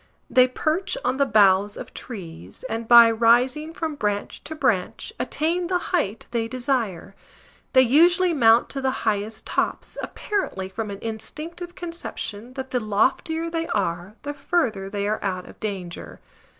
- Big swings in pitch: Yes, wide, 7.0 semitones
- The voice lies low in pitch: No, high, 240 Hz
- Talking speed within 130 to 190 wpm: Yes, average, 155 wpm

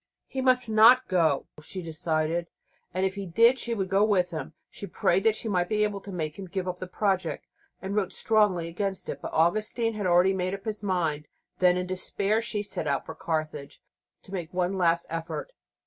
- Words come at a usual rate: No, fast, 210 wpm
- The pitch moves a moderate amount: Yes, average, 3.5 semitones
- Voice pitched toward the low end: No, medium, 185 Hz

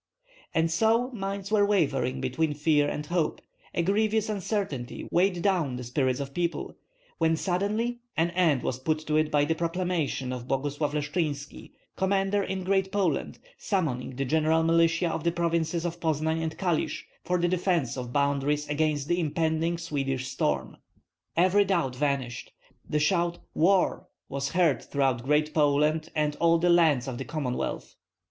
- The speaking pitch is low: No, medium, 160 Hz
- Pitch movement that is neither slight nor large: Yes, average, 3.9 semitones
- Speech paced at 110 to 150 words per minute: No, average, 160 wpm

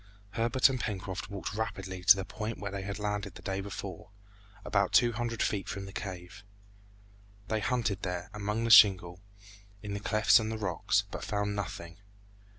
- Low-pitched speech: Yes, low, 100 Hz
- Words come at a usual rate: Yes, average, 175 wpm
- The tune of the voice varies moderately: No, narrow, 2.2 semitones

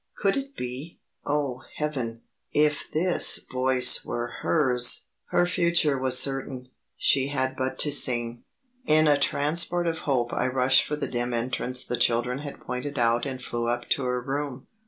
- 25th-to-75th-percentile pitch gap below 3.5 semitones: Yes, average, 3.0 semitones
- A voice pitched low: Yes, low, 130 Hz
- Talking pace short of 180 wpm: Yes, average, 165 wpm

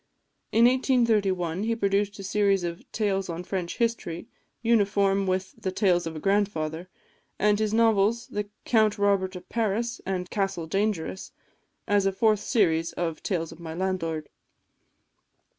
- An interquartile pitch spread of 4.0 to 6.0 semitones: No, average, 3.1 semitones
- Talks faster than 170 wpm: No, average, 140 wpm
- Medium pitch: No, high, 195 Hz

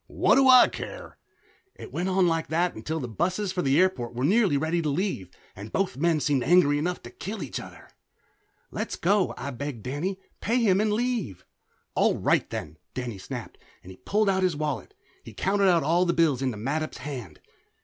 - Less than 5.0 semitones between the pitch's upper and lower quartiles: No, wide, 5.6 semitones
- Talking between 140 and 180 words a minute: No, average, 195 wpm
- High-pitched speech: No, medium, 165 Hz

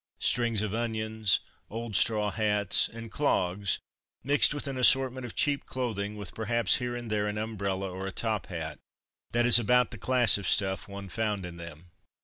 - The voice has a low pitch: Yes, low, 110 Hz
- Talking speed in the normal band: Yes, average, 180 wpm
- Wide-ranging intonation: No, average, 3.3 semitones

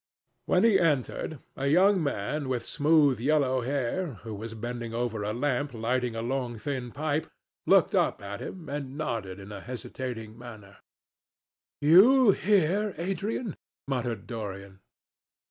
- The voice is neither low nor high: No, low, 130 Hz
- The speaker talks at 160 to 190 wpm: No, average, 140 wpm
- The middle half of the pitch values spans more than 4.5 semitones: Yes, average, 5.3 semitones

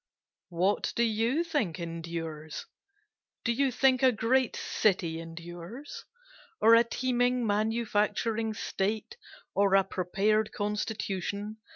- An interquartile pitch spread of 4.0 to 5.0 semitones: Yes, average, 4.4 semitones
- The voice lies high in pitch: Yes, high, 215 Hz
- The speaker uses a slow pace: Yes, slow, 105 wpm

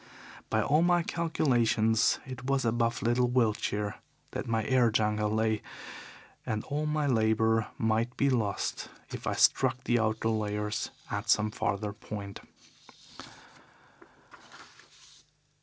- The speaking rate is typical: No, slow, 120 wpm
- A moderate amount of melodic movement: Yes, average, 3.0 semitones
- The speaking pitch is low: Yes, low, 115 Hz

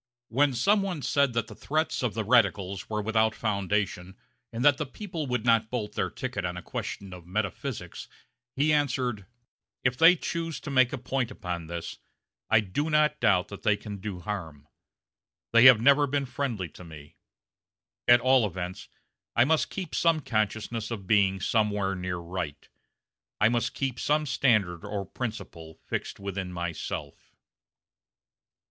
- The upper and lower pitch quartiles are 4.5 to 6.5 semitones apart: Yes, wide, 5.6 semitones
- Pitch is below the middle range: Yes, low, 110 Hz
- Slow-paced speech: No, average, 160 wpm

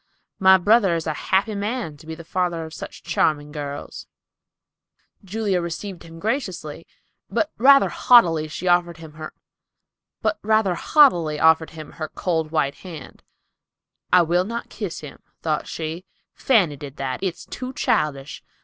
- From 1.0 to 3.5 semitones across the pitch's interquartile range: No, average, 4.3 semitones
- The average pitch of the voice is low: No, medium, 170 Hz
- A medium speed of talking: No, slow, 125 wpm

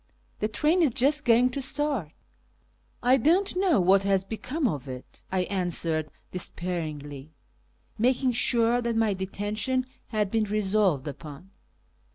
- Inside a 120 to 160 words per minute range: Yes, average, 145 wpm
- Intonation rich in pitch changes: Yes, wide, 6.0 semitones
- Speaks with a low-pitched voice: No, high, 215 Hz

